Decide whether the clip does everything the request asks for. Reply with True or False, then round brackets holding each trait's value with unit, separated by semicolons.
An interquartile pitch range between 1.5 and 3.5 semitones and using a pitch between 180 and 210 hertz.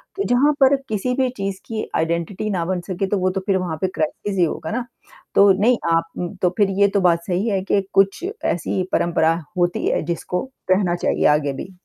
True (2.9 semitones; 190 Hz)